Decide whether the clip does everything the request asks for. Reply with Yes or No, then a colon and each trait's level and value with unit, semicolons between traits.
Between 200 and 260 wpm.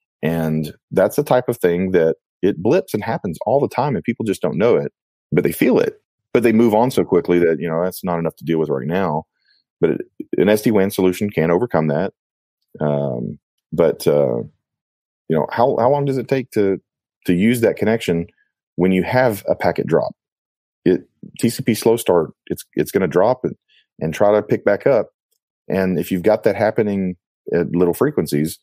Yes: fast, 205 wpm